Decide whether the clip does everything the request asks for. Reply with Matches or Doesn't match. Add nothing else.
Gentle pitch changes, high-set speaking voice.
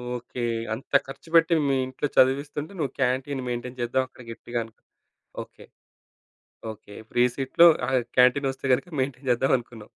Doesn't match